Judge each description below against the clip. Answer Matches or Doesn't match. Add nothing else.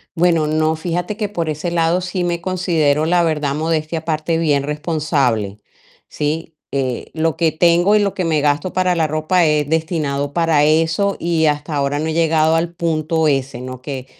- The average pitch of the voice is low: Doesn't match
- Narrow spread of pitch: Matches